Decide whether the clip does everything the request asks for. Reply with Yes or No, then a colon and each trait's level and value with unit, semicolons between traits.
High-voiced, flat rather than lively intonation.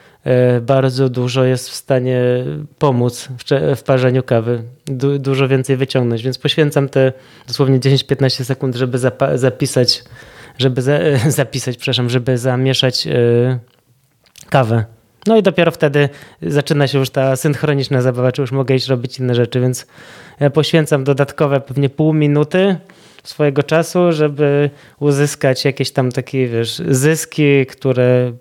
No: low, 135 Hz; narrow, 2.3 semitones